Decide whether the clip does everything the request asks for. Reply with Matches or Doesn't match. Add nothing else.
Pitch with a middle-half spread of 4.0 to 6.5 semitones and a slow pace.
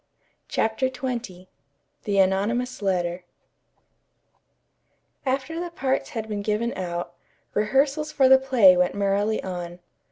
Matches